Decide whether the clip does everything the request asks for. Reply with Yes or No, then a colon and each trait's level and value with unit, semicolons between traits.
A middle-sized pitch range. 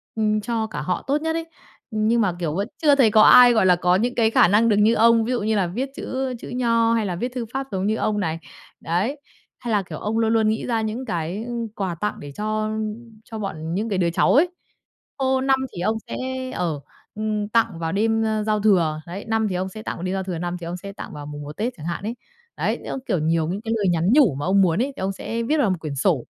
Yes: average, 4.4 semitones